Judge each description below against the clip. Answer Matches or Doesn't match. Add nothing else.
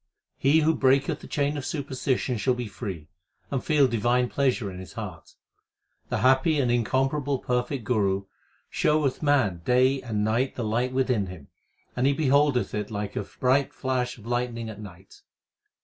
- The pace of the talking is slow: Doesn't match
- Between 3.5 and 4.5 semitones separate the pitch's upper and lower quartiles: Matches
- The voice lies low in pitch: Matches